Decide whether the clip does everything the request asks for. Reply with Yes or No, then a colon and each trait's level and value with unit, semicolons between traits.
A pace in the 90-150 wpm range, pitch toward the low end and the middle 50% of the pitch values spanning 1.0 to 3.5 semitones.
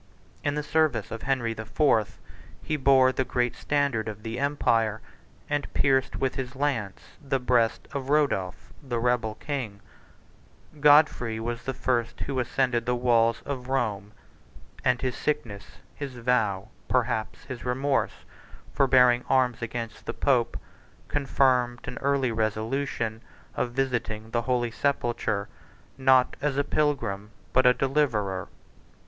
Yes: average, 140 wpm; low, 125 Hz; average, 3.1 semitones